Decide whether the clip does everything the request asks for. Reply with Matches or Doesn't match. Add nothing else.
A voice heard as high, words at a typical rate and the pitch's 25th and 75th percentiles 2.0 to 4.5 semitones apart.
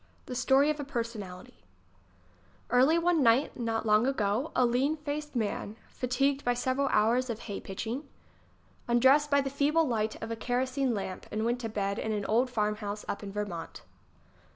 Matches